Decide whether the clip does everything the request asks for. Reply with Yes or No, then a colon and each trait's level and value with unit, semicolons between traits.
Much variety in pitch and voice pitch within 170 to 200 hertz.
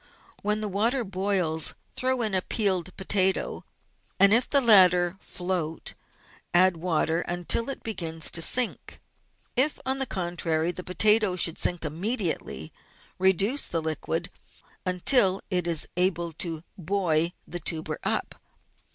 No: average, 3.8 semitones; medium, 185 Hz